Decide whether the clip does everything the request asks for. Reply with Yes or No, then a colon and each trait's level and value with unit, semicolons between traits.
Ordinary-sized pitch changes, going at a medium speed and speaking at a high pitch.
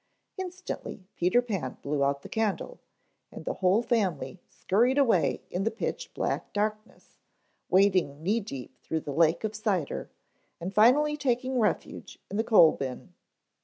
No: wide, 5.8 semitones; average, 150 wpm; high, 205 Hz